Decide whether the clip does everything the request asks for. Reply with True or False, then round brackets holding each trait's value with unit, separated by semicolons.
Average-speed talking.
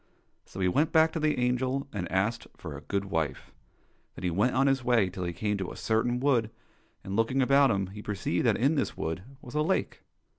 False (225 wpm)